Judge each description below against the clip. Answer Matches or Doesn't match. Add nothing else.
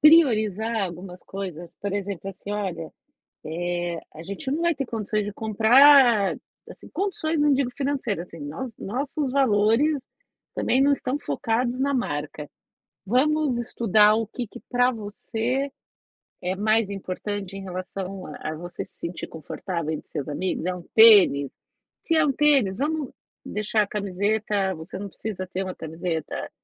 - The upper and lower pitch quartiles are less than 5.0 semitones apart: Doesn't match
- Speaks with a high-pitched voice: Matches